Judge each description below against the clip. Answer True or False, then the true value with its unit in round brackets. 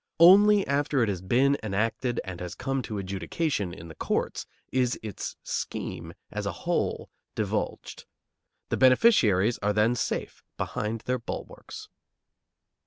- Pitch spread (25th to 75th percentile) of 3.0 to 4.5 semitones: False (5.1 semitones)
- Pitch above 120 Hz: False (115 Hz)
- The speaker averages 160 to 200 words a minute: False (135 wpm)